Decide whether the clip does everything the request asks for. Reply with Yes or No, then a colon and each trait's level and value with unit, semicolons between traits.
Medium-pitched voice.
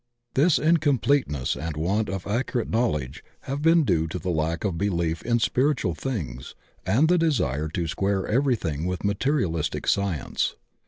No: low, 100 Hz